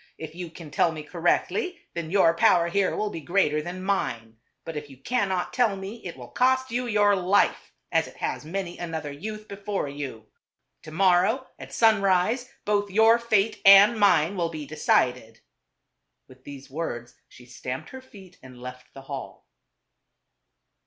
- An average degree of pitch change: No, wide, 5.7 semitones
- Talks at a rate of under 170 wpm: No, average, 175 wpm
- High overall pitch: No, medium, 175 Hz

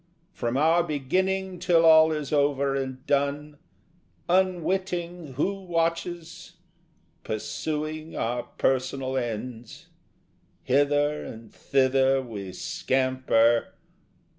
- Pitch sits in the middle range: Yes, medium, 145 Hz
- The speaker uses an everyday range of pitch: Yes, average, 4.3 semitones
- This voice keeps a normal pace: No, slow, 90 wpm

